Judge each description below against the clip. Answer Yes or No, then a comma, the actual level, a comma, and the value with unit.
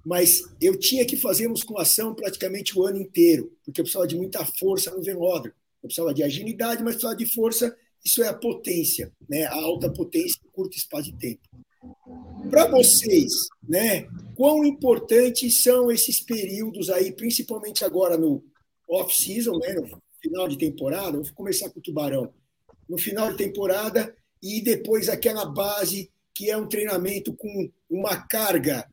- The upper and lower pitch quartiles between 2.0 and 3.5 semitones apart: No, average, 4.8 semitones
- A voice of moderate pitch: No, high, 215 Hz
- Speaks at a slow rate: No, average, 165 wpm